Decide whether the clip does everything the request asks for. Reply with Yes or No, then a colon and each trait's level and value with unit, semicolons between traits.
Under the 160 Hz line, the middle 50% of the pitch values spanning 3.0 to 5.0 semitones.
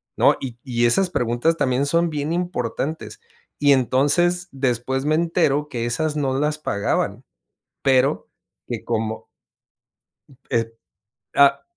Yes: medium, 140 Hz; average, 4.1 semitones